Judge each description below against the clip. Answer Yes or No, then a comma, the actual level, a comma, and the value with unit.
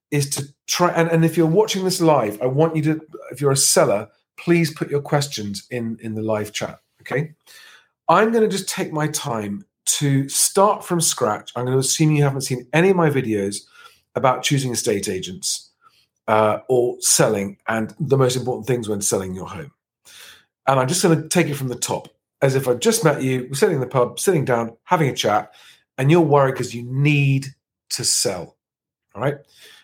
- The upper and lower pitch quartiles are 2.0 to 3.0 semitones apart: No, average, 4.9 semitones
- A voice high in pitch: No, medium, 140 Hz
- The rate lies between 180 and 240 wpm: Yes, fast, 205 wpm